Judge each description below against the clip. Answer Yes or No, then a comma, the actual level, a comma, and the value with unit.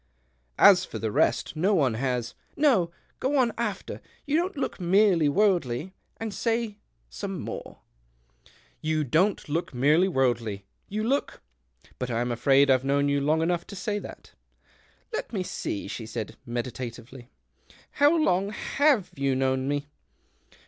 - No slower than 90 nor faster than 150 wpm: No, average, 170 wpm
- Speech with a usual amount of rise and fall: No, wide, 8.3 semitones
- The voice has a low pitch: No, medium, 155 Hz